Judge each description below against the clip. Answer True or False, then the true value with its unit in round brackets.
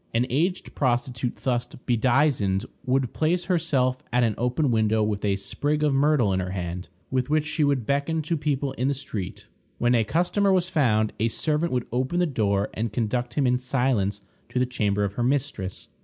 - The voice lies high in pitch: False (125 Hz)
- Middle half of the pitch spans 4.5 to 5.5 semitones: True (4.9 semitones)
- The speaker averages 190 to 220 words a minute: True (195 wpm)